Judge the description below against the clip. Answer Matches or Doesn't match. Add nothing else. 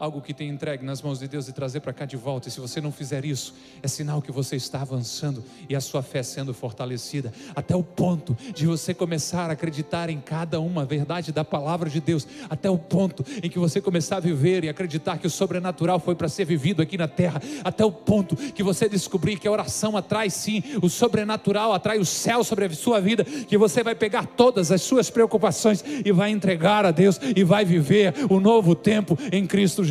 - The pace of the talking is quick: Matches